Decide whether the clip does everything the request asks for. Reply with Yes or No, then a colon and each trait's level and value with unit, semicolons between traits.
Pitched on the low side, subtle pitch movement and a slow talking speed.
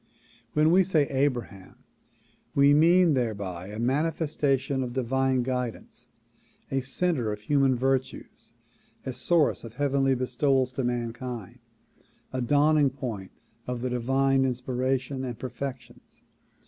Yes: low, 130 Hz; narrow, 2.3 semitones; slow, 115 wpm